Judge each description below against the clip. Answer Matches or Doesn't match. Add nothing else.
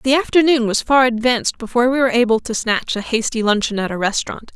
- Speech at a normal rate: Doesn't match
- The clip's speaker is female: Matches